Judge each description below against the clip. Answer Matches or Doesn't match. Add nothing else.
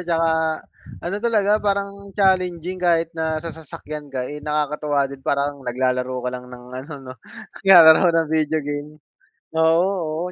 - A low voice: Doesn't match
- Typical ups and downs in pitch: Matches